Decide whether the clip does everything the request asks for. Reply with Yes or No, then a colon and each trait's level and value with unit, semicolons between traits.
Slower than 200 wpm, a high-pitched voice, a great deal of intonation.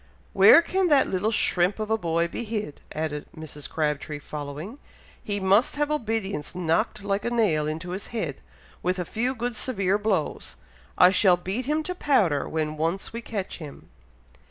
Yes: average, 175 wpm; high, 195 Hz; wide, 6.0 semitones